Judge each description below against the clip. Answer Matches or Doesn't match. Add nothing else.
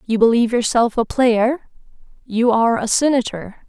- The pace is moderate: Matches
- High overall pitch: Matches